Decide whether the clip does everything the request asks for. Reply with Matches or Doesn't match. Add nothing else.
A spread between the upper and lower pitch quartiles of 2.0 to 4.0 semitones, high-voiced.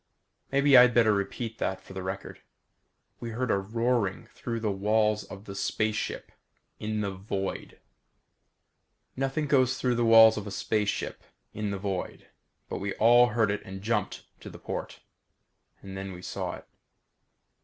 Doesn't match